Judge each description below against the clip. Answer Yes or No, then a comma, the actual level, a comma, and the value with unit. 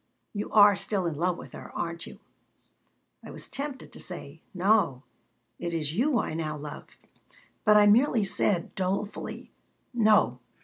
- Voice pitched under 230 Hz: Yes, high, 190 Hz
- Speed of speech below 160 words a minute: Yes, average, 150 wpm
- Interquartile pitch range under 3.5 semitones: No, average, 4.2 semitones